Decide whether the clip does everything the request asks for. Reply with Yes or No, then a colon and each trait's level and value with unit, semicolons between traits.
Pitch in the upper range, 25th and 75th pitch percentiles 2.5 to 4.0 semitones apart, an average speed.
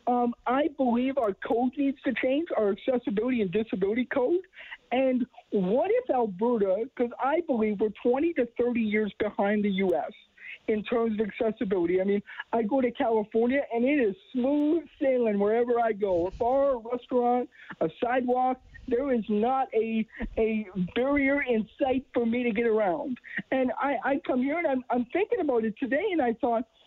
Yes: high, 245 Hz; average, 3.1 semitones; average, 180 wpm